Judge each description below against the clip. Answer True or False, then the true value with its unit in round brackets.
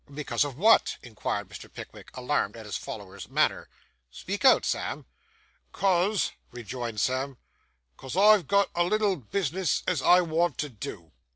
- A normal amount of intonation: False (7.6 semitones)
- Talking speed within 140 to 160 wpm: True (150 wpm)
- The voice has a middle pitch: True (150 Hz)